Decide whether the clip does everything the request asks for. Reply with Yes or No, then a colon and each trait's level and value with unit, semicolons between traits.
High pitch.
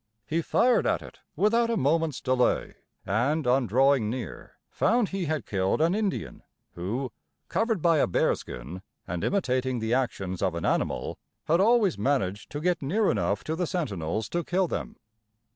No: medium, 140 Hz